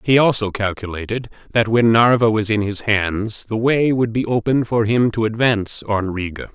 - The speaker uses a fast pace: No, average, 195 wpm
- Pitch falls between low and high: No, low, 110 Hz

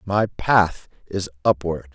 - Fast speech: No, slow, 125 wpm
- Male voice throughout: Yes, male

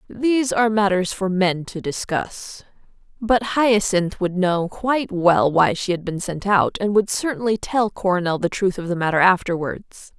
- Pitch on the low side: No, high, 195 Hz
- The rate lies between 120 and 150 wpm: No, average, 175 wpm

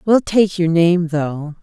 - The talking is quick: No, average, 185 wpm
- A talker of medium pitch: Yes, medium, 175 Hz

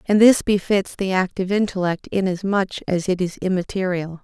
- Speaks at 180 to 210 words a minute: No, average, 155 wpm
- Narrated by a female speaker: Yes, female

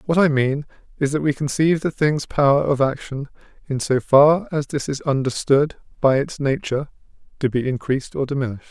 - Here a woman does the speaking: No, male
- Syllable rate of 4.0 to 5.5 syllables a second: No, 5.7 syllables/s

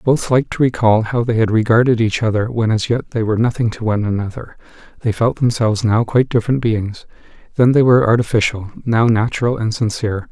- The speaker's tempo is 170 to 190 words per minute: No, average, 200 wpm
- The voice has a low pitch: Yes, low, 115 Hz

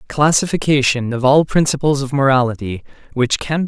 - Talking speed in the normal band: Yes, average, 145 wpm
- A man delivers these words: Yes, male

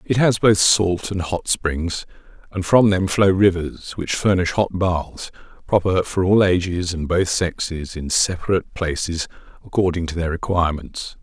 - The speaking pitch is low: Yes, very low, 90 Hz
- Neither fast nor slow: Yes, average, 160 wpm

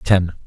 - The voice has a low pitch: Yes, very low, 90 Hz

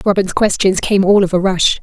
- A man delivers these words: No, female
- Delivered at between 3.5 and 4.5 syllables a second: No, 5.2 syllables/s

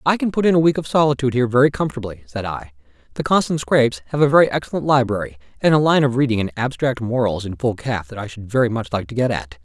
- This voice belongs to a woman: No, male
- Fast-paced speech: Yes, fast, 255 wpm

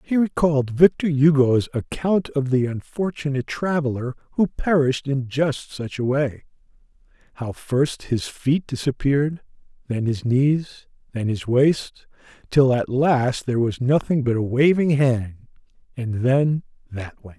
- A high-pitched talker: No, low, 135 Hz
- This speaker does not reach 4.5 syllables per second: Yes, 4.3 syllables/s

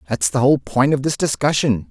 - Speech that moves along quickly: Yes, fast, 220 wpm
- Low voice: Yes, low, 125 Hz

